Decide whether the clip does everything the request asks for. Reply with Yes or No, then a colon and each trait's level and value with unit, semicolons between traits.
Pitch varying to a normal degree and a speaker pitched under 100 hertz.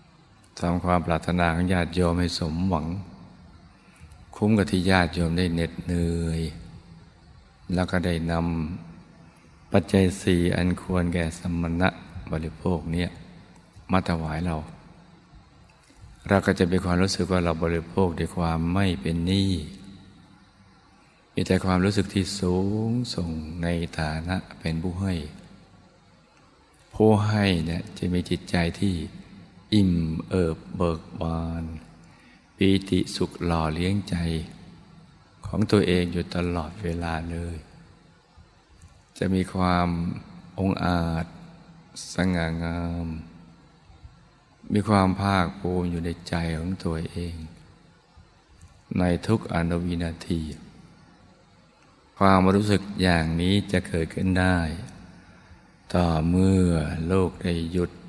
No: narrow, 1.9 semitones; very low, 90 Hz